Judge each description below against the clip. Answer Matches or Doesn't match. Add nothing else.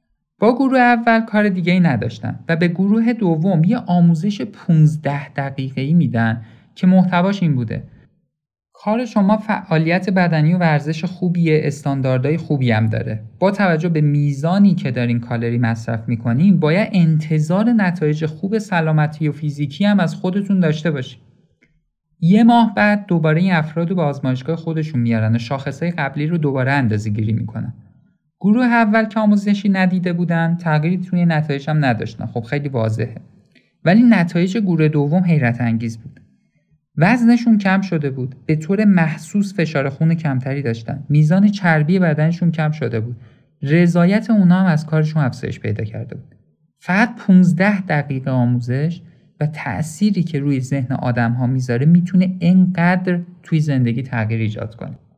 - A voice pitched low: Doesn't match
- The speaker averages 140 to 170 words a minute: Matches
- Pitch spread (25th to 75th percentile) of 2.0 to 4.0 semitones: Doesn't match